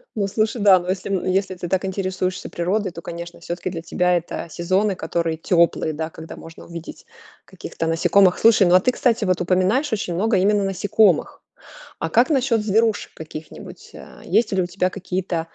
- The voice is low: No, medium, 185 Hz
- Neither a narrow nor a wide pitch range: Yes, average, 3.0 semitones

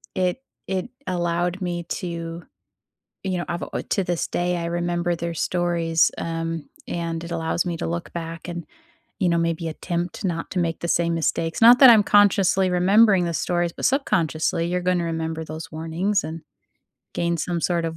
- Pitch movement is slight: Yes, narrow, 1.4 semitones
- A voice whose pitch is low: No, medium, 170 Hz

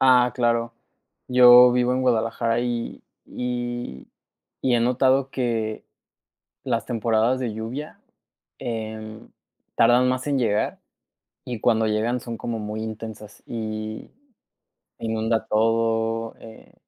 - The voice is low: Yes, low, 115 Hz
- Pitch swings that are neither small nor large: No, narrow, 1.9 semitones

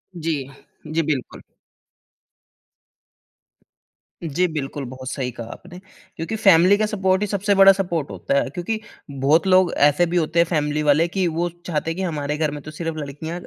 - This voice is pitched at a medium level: Yes, medium, 165 Hz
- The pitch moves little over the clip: No, average, 3.8 semitones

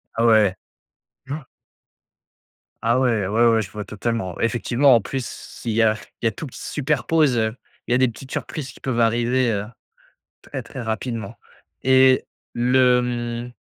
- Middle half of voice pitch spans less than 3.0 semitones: Yes, narrow, 2.6 semitones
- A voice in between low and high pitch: No, low, 120 Hz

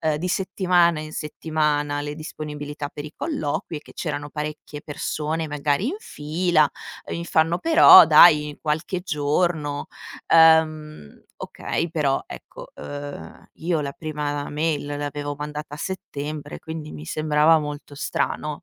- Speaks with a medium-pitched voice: Yes, medium, 150 Hz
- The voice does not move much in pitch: Yes, narrow, 1.7 semitones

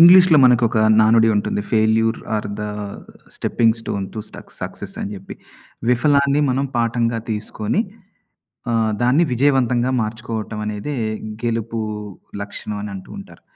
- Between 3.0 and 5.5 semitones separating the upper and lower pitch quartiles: No, narrow, 2.6 semitones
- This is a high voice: No, low, 115 Hz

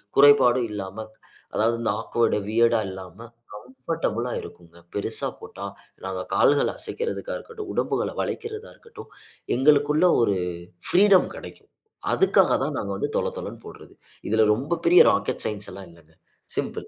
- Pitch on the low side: Yes, low, 120 Hz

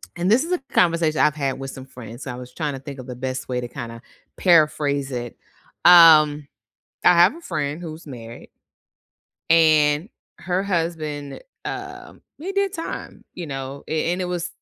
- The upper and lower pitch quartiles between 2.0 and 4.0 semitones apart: No, average, 4.5 semitones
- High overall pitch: No, medium, 150 Hz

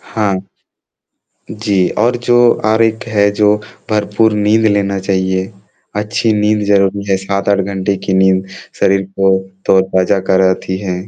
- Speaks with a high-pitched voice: No, low, 100 Hz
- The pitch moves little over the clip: Yes, narrow, 1.9 semitones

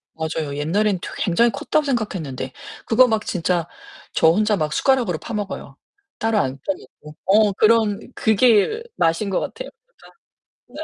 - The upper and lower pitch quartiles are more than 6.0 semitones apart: No, wide, 5.4 semitones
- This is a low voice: No, high, 205 Hz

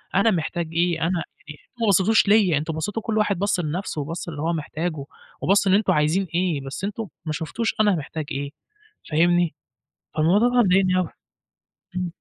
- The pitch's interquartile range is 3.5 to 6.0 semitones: Yes, average, 4.1 semitones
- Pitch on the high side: No, medium, 175 Hz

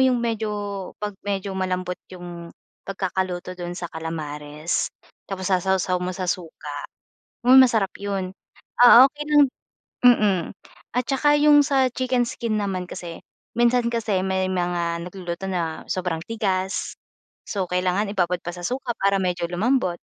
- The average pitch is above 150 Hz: Yes, high, 190 Hz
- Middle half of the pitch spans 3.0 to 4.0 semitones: No, average, 4.4 semitones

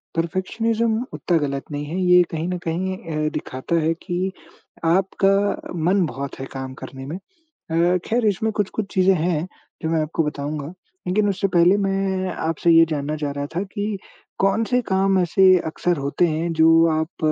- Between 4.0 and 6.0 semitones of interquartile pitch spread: No, average, 3.6 semitones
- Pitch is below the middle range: No, medium, 175 Hz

